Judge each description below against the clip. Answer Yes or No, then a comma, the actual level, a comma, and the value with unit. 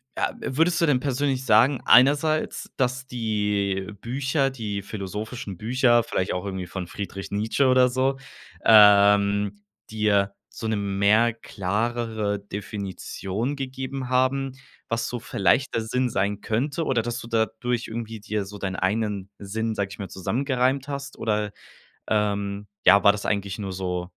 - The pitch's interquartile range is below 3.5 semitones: No, average, 4.0 semitones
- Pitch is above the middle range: No, low, 110 Hz